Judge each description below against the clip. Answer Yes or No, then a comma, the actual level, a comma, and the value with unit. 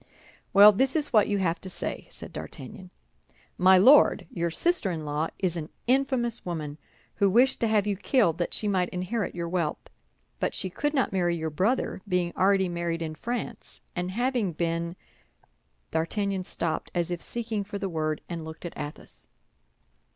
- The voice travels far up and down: No, average, 4.4 semitones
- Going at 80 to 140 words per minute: No, average, 175 wpm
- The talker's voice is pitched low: No, medium, 185 Hz